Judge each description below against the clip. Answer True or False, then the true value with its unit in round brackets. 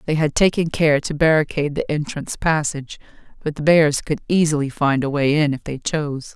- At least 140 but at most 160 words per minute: False (200 wpm)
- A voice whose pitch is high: False (150 Hz)